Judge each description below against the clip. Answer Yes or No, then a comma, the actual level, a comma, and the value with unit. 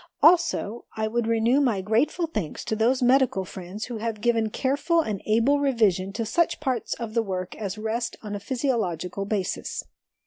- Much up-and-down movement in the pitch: No, average, 3.8 semitones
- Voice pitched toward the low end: No, high, 225 Hz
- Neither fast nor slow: Yes, average, 175 wpm